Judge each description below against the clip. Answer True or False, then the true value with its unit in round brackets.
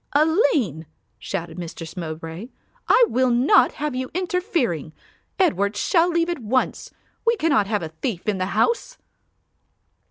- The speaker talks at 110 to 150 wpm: True (135 wpm)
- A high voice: True (240 Hz)